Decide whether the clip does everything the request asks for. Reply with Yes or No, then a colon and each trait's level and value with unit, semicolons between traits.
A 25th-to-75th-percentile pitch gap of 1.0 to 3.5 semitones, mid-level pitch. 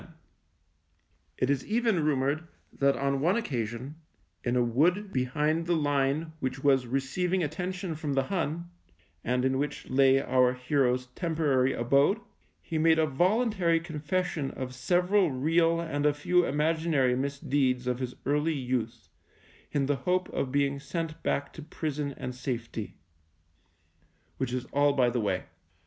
No: average, 4.1 semitones; medium, 145 Hz